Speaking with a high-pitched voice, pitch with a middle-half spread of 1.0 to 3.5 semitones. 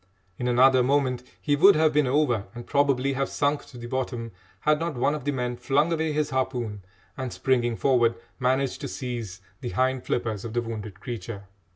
No: low, 130 Hz; average, 3.1 semitones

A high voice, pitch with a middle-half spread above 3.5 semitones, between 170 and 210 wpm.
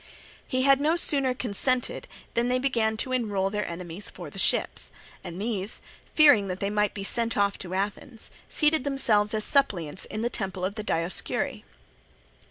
Yes: high, 215 Hz; average, 4.5 semitones; average, 175 wpm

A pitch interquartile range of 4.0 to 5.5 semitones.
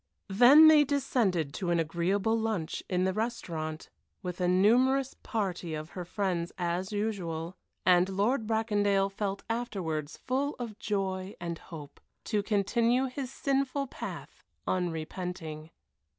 Yes: average, 5.0 semitones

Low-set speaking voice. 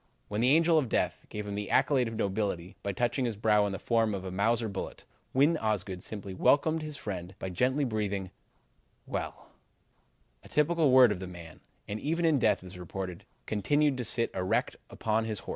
Yes: low, 110 Hz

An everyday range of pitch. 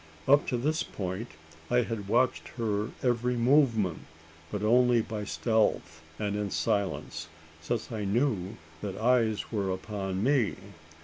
Yes: average, 3.4 semitones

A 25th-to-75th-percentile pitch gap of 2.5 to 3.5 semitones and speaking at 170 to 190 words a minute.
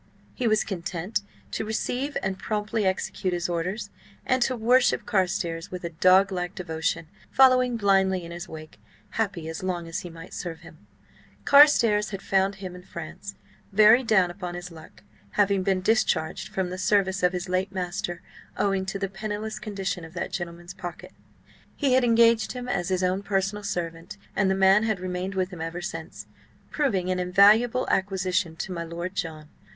Yes: average, 2.9 semitones; average, 175 wpm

